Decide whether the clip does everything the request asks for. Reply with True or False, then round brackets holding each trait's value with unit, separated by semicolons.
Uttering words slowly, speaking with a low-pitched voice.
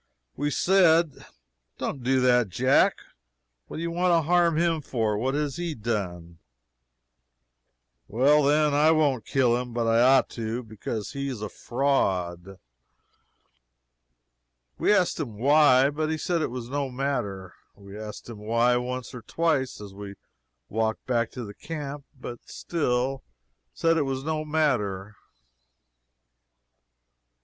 False (145 wpm; 130 Hz)